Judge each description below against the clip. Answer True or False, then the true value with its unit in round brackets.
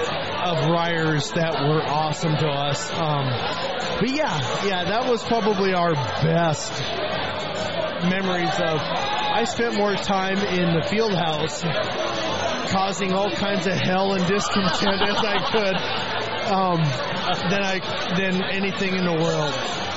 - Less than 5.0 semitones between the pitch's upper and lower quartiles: True (3.4 semitones)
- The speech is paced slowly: True (130 wpm)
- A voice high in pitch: False (180 Hz)